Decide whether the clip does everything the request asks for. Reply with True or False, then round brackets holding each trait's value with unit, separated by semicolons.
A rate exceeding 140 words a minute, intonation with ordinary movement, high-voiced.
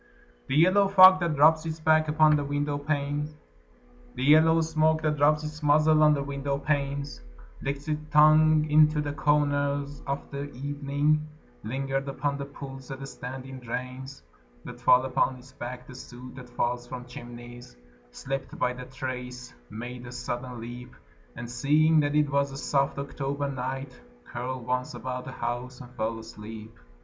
False (165 wpm; 3.0 semitones; 140 Hz)